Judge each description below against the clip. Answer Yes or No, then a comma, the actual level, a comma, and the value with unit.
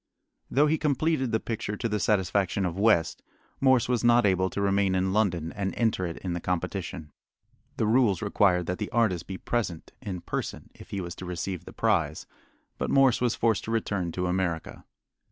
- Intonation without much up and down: No, average, 4.0 semitones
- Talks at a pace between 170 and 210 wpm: Yes, average, 190 wpm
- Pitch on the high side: No, low, 100 Hz